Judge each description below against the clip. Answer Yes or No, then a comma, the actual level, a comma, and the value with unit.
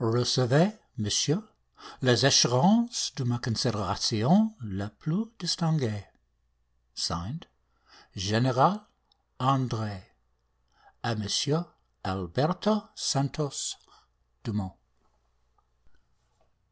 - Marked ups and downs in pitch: Yes, wide, 7.2 semitones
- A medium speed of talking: No, slow, 65 wpm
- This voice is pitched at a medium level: No, low, 125 Hz